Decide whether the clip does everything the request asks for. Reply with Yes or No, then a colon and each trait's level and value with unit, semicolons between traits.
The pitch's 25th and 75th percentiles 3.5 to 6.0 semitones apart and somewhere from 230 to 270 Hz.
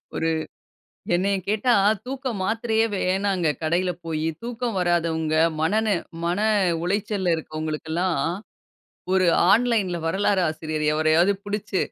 No: average, 4.3 semitones; medium, 185 Hz